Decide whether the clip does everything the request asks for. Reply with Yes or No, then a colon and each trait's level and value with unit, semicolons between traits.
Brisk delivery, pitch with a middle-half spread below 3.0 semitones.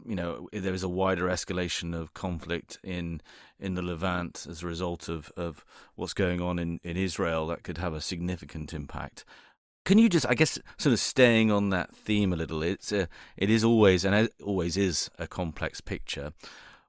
No: average, 195 wpm; narrow, 2.6 semitones